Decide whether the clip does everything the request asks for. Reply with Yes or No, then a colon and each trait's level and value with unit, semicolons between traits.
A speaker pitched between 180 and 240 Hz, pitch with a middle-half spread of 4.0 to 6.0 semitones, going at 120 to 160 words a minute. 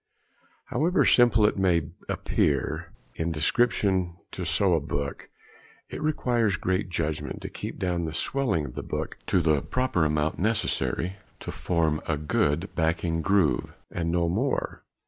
No: very low, 85 Hz; average, 4.3 semitones; average, 145 wpm